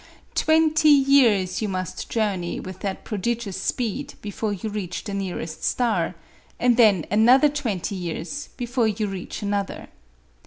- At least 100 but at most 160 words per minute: Yes, average, 140 wpm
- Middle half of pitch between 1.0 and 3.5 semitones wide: No, average, 4.5 semitones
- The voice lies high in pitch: Yes, high, 210 Hz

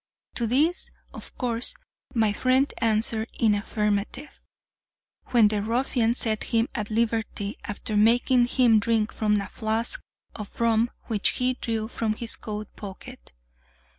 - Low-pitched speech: No, high, 225 Hz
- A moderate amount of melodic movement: No, narrow, 2.0 semitones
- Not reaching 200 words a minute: Yes, average, 140 wpm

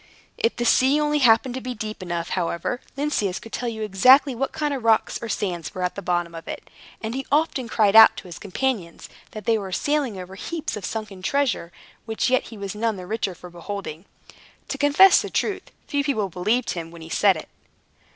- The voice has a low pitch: No, high, 220 Hz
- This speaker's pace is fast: Yes, fast, 215 wpm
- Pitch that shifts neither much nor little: No, wide, 5.9 semitones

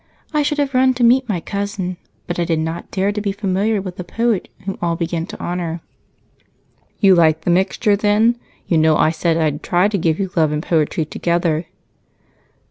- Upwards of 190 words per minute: Yes, average, 200 wpm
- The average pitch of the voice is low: No, medium, 180 Hz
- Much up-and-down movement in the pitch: No, average, 3.8 semitones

